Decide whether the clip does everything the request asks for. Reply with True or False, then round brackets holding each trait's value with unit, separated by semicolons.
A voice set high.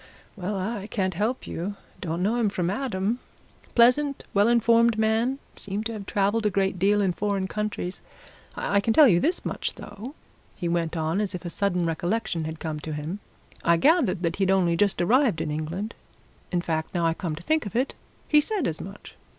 True (200 Hz)